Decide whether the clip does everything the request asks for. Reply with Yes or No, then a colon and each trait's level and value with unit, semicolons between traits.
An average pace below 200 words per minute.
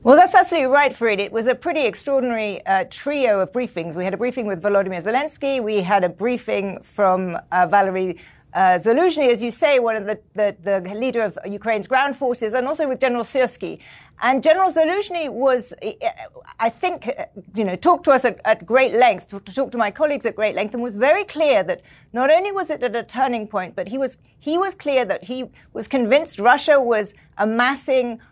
No: fast, 205 wpm